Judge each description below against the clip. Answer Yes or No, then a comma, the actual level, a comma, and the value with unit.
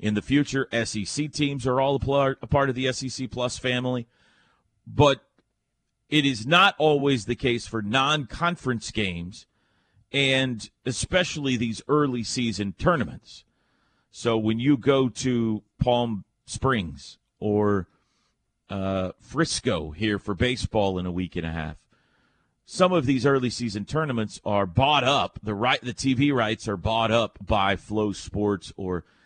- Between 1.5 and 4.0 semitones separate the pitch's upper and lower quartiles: No, average, 4.4 semitones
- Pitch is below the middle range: Yes, low, 120 Hz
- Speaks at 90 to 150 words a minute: Yes, average, 145 wpm